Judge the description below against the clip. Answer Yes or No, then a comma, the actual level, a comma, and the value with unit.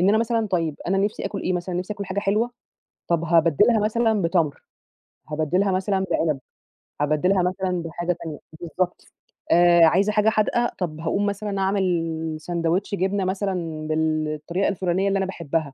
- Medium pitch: Yes, medium, 180 Hz